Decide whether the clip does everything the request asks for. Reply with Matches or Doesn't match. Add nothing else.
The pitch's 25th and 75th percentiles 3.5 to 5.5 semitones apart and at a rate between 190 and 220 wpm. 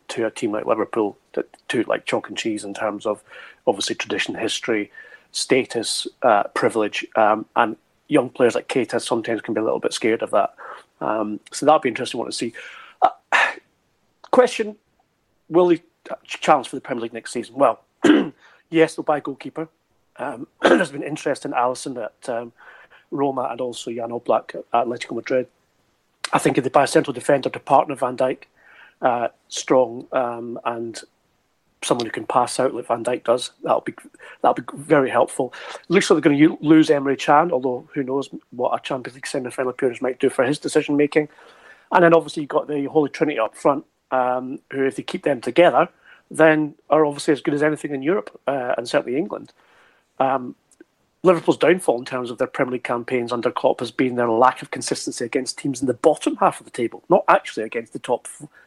Matches